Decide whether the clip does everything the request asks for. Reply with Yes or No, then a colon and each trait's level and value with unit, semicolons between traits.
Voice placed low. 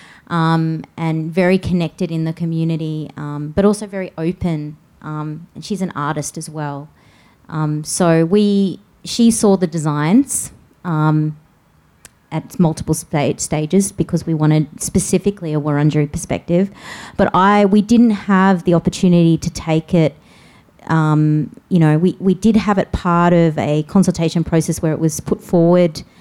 No: medium, 165 Hz